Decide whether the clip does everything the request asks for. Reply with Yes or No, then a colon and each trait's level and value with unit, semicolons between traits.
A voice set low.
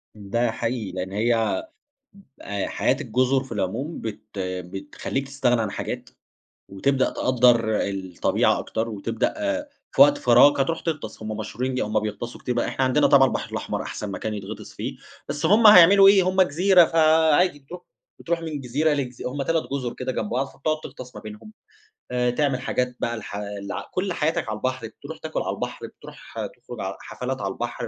Yes: low, 125 Hz